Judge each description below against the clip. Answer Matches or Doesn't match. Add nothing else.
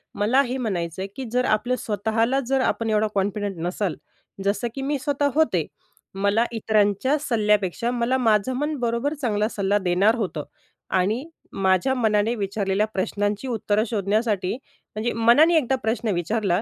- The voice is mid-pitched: Doesn't match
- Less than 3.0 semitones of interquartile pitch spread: Doesn't match